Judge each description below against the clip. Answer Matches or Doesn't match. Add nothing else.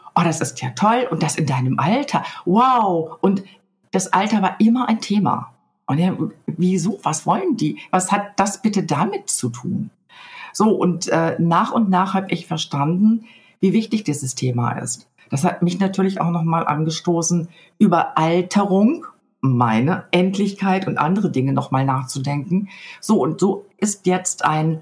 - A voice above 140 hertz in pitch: Matches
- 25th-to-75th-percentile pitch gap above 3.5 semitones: Matches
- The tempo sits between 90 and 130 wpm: Doesn't match